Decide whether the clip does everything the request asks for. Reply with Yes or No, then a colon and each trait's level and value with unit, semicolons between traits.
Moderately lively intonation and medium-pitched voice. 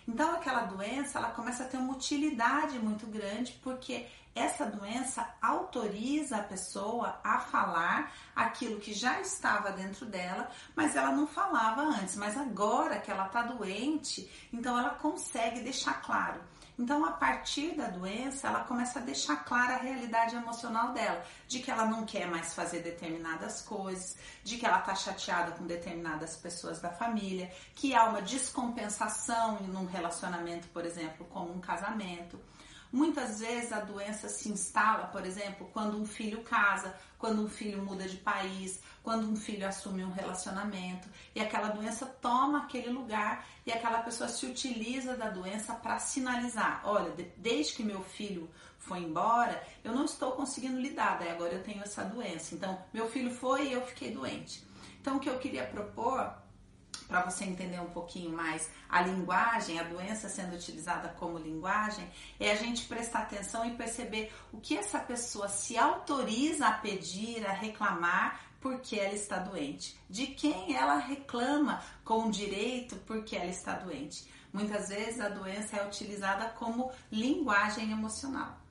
No: average, 4.3 semitones; high, 220 Hz